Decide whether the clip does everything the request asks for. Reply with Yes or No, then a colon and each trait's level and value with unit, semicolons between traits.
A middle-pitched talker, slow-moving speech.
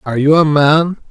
No: medium, 150 Hz; fast, 220 wpm